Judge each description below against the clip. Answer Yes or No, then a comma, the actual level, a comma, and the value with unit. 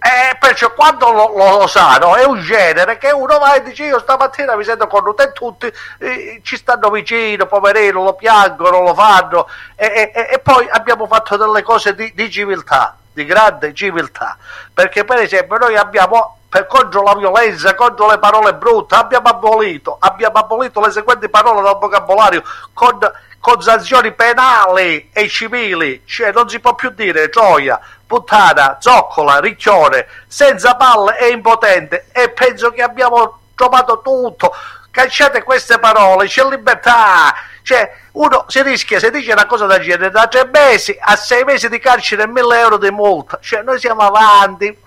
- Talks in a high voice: Yes, high, 230 Hz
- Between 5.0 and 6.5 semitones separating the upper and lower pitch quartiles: No, average, 3.7 semitones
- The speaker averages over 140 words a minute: Yes, fast, 170 wpm